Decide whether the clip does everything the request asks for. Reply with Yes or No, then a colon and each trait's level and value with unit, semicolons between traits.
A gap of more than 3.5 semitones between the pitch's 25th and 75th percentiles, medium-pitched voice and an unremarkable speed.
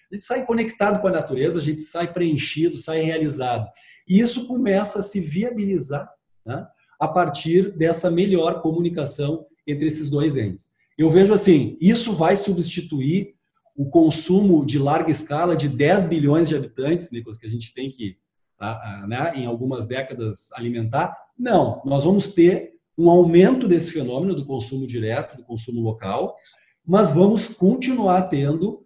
Yes: average, 5.2 semitones; medium, 165 Hz; average, 155 wpm